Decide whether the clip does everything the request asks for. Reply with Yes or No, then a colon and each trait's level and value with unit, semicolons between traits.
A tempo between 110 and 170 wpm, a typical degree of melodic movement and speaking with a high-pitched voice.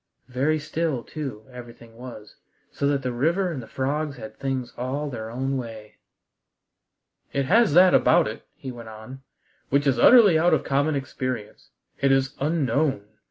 No: average, 160 wpm; average, 3.8 semitones; low, 135 Hz